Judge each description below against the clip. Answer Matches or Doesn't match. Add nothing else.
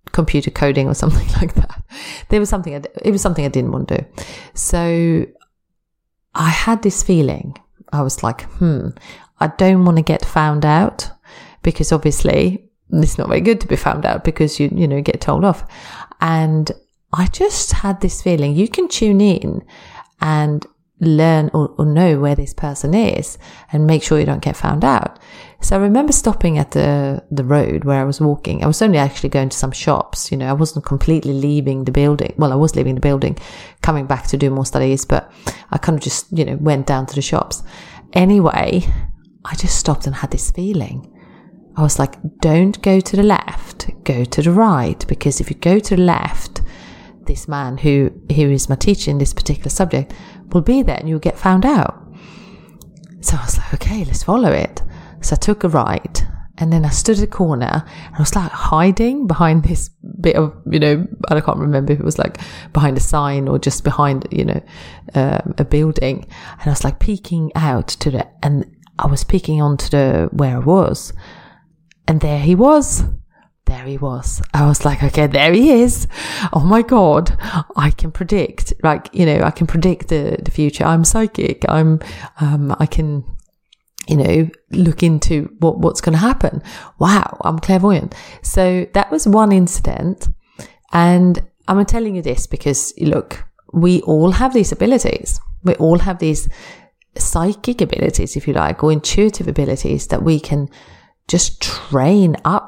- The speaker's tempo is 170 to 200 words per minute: Matches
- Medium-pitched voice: Matches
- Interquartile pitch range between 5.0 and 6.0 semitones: Doesn't match